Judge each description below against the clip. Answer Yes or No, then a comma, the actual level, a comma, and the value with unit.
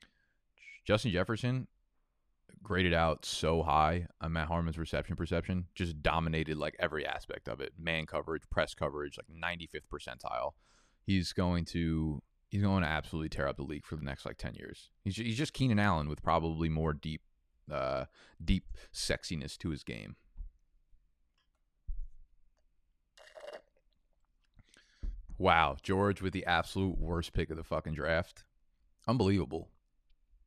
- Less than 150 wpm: Yes, slow, 135 wpm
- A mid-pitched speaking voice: No, very low, 80 Hz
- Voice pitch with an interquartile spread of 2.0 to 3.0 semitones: No, average, 3.4 semitones